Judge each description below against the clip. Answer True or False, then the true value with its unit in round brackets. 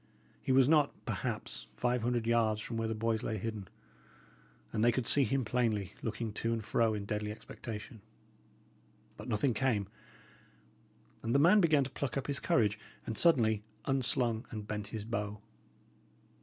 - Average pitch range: True (3.1 semitones)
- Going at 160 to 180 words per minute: True (165 wpm)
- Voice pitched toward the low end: True (115 Hz)